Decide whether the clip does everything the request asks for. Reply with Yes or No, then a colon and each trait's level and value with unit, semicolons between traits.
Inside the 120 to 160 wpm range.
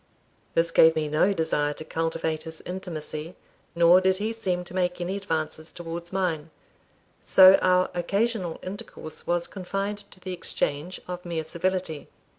Yes: average, 150 wpm